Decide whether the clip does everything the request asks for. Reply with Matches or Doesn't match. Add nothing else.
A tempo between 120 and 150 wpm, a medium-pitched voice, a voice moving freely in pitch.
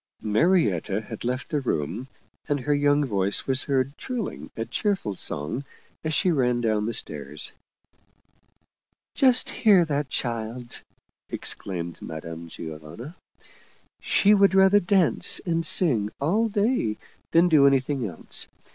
Doesn't match